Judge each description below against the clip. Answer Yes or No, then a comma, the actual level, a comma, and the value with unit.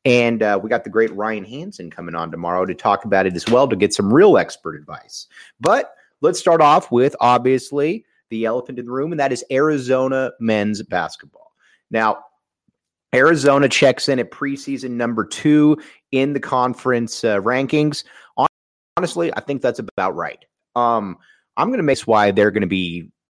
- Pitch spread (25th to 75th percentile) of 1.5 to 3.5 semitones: No, average, 4.4 semitones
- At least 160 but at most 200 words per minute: Yes, average, 180 wpm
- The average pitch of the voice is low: Yes, low, 125 Hz